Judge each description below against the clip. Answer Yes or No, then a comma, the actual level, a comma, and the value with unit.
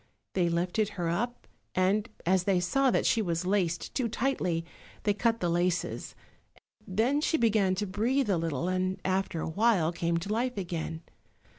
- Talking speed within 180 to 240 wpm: No, average, 170 wpm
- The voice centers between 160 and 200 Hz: Yes, medium, 185 Hz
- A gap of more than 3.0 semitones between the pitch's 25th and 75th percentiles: Yes, average, 4.2 semitones